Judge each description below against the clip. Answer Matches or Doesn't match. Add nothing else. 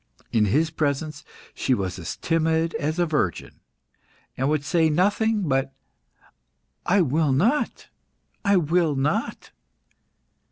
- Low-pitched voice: Doesn't match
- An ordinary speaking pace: Doesn't match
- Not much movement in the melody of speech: Doesn't match